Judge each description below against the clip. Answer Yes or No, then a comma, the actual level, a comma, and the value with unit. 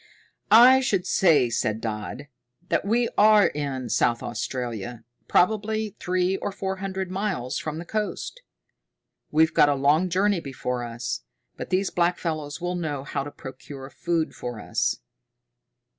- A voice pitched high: No, medium, 160 Hz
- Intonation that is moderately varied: No, wide, 6.6 semitones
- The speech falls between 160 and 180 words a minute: No, average, 145 wpm